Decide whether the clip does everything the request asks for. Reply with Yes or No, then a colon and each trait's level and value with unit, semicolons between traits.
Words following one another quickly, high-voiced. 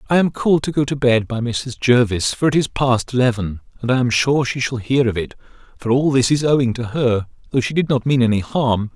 No: fast, 255 wpm; low, 125 Hz